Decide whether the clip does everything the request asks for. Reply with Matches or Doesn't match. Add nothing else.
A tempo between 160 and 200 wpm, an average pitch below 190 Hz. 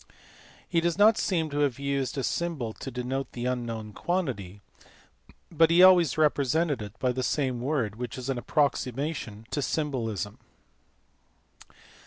Doesn't match